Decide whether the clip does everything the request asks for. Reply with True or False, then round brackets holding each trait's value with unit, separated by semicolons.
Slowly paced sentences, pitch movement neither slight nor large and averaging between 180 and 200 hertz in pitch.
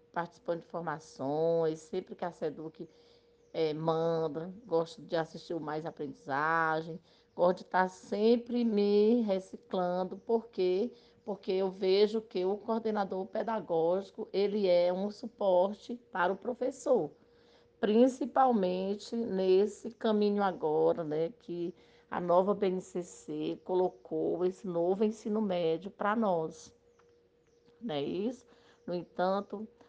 True (115 wpm; 4.3 semitones; 190 Hz)